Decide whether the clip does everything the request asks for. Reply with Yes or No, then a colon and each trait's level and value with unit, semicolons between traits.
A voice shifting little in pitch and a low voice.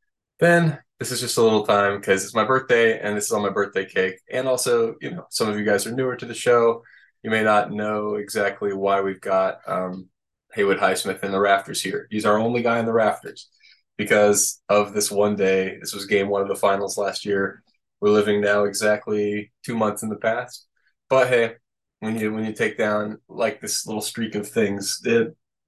Yes: narrow, 2.3 semitones; low, 105 Hz